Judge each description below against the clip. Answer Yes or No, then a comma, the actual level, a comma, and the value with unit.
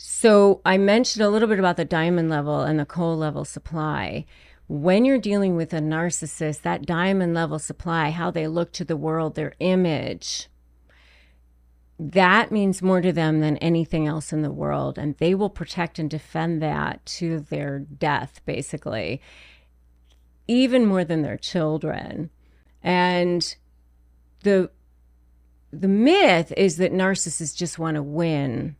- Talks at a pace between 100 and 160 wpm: Yes, average, 150 wpm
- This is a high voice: No, medium, 160 Hz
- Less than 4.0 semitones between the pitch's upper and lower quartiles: No, average, 4.8 semitones